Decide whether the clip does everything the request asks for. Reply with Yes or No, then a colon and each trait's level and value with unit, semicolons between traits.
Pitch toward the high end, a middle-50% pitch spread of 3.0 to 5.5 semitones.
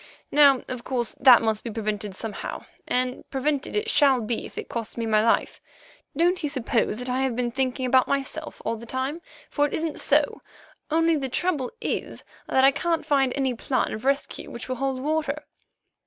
Yes: very high, 260 Hz; average, 3.4 semitones